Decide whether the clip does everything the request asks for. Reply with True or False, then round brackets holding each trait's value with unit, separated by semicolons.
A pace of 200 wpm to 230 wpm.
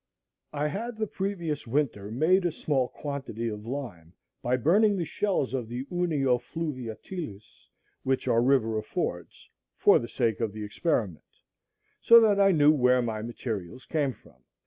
False (155 wpm)